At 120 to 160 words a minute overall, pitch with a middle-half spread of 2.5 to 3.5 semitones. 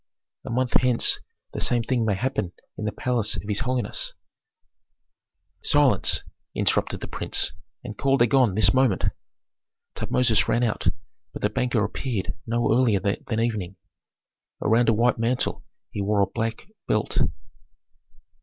Yes: average, 145 wpm; average, 3.2 semitones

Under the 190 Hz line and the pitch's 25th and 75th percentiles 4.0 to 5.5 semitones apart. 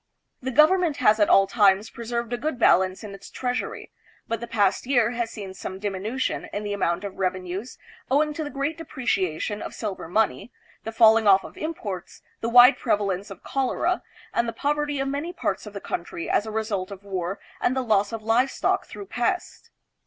No: high, 220 Hz; average, 4.7 semitones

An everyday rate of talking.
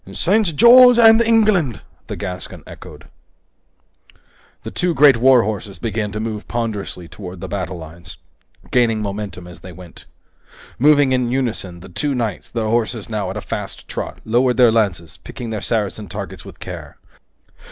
Yes: average, 160 wpm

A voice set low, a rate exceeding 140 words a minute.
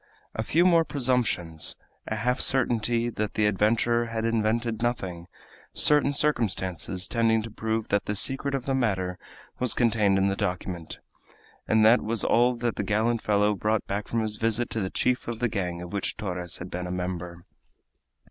Yes: low, 110 Hz; average, 180 wpm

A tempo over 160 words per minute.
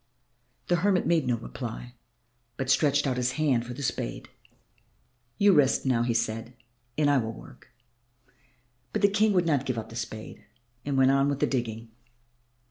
Yes: average, 175 wpm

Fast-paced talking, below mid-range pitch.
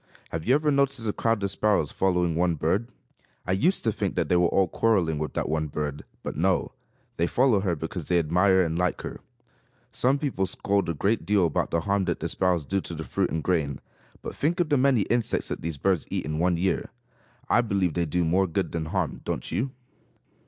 Yes: fast, 225 wpm; very low, 90 Hz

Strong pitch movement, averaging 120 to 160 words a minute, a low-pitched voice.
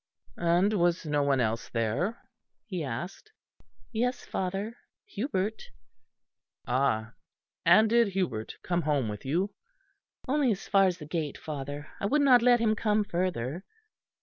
No: wide, 7.0 semitones; average, 140 wpm; medium, 180 Hz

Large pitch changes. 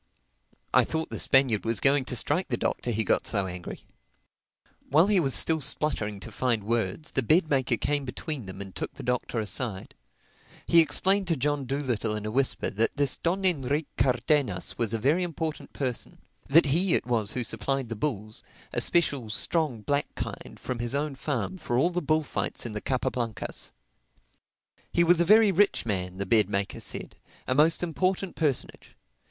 Yes: wide, 5.7 semitones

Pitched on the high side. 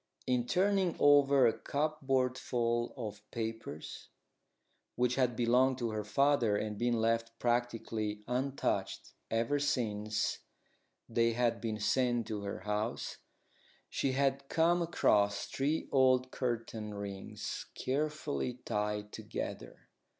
No: low, 120 Hz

